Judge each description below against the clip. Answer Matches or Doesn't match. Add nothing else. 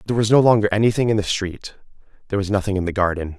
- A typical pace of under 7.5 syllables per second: Doesn't match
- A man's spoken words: Matches